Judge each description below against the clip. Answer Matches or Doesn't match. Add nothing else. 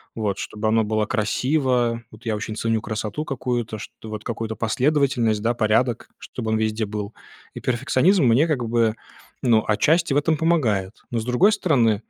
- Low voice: Matches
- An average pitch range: Matches